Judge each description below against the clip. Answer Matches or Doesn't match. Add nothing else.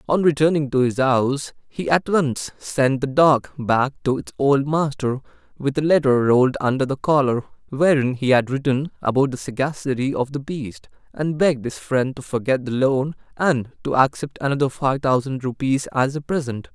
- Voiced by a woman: Doesn't match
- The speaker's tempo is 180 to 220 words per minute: Matches